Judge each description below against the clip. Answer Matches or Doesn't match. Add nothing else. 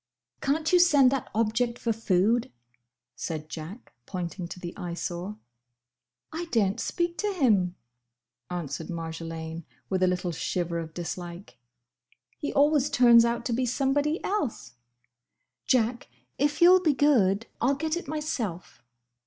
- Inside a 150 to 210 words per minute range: Doesn't match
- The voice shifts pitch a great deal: Matches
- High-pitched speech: Matches